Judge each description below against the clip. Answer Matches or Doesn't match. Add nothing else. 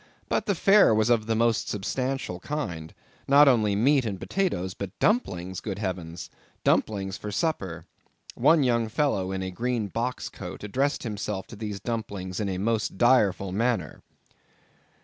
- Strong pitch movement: Doesn't match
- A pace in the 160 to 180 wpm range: Doesn't match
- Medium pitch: Doesn't match